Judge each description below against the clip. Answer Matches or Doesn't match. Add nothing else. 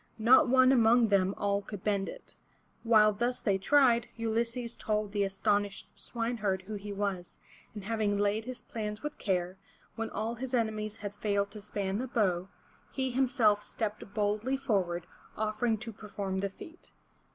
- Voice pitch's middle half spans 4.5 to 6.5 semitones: Doesn't match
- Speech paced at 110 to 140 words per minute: Doesn't match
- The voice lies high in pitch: Matches